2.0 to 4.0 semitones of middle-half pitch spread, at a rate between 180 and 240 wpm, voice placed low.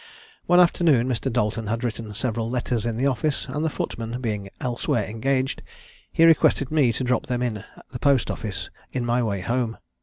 Yes: average, 2.9 semitones; average, 185 wpm; low, 120 Hz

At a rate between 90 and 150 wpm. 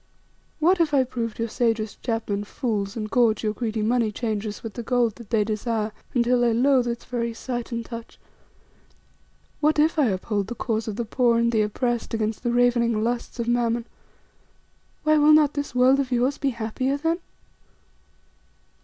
No: average, 175 wpm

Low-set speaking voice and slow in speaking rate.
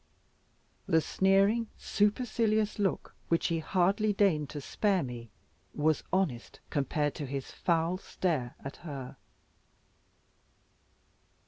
No: medium, 170 Hz; slow, 105 wpm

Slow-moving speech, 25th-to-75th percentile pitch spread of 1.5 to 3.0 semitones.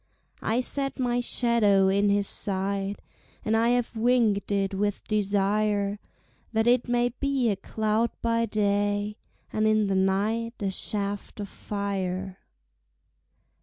Yes: slow, 130 wpm; narrow, 2.5 semitones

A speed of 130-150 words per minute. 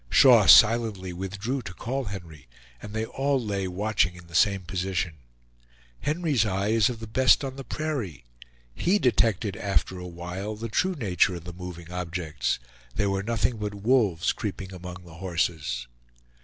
No: average, 165 wpm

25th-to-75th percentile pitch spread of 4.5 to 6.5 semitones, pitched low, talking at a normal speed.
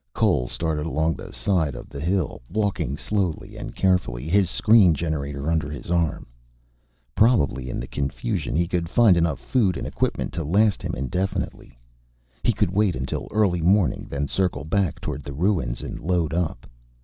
Yes: average, 4.9 semitones; very low, 85 Hz; average, 170 wpm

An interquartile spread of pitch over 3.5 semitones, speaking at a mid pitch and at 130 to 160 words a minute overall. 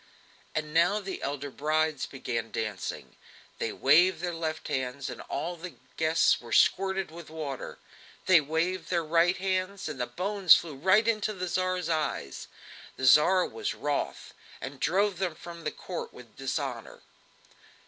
Yes: average, 4.4 semitones; medium, 165 Hz; average, 150 wpm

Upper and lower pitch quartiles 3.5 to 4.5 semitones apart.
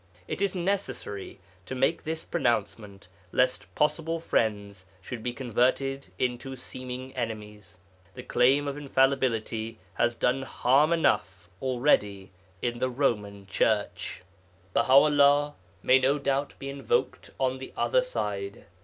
Yes: average, 4.0 semitones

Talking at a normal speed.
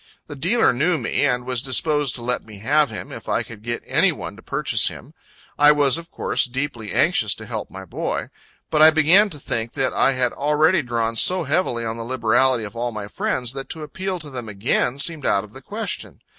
No: fast, 225 wpm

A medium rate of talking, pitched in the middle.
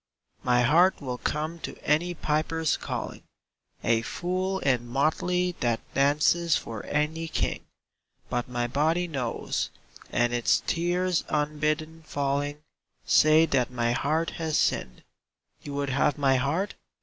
No: slow, 130 wpm; medium, 150 Hz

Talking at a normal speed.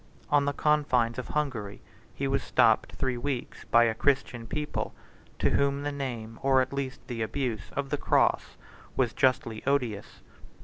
Yes: average, 165 wpm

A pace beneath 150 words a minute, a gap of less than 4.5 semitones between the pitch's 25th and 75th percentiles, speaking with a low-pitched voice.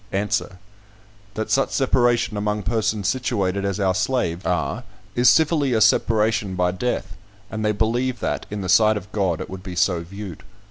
No: average, 175 wpm; average, 3.5 semitones; low, 105 Hz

